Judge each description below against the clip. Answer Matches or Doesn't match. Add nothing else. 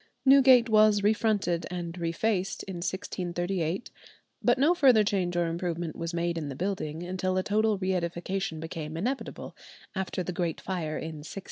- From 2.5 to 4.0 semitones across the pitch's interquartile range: Matches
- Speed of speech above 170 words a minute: Doesn't match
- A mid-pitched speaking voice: Matches